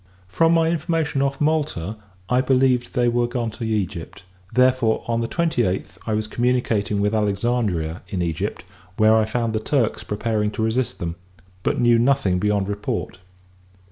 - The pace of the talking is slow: No, average, 165 wpm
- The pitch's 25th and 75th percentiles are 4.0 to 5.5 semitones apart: No, average, 3.6 semitones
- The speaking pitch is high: No, low, 115 Hz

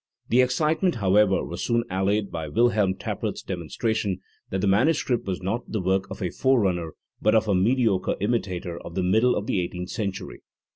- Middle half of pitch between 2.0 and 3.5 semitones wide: No, average, 4.0 semitones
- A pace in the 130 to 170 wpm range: No, average, 180 wpm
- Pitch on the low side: Yes, low, 100 Hz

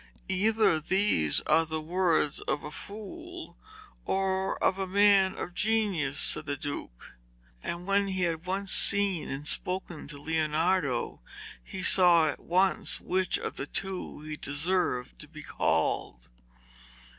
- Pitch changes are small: No, average, 4.1 semitones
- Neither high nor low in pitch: Yes, medium, 180 Hz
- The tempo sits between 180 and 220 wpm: No, average, 140 wpm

